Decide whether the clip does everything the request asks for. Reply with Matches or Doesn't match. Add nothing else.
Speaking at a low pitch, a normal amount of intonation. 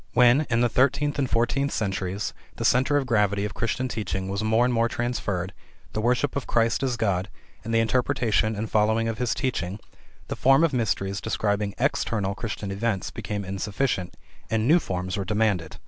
Matches